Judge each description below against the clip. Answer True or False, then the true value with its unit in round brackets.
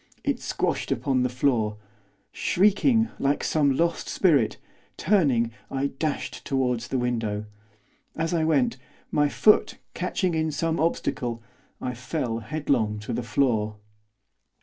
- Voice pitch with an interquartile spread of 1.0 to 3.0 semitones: False (5.3 semitones)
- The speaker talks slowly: True (125 wpm)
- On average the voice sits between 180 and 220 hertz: False (140 Hz)